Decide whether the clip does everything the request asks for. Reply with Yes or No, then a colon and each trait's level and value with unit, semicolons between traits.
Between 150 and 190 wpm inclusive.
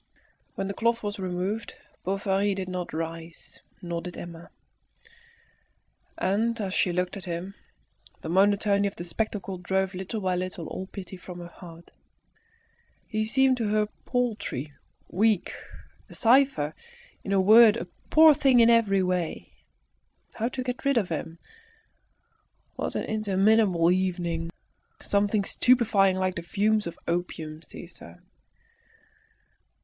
No: slow, 135 wpm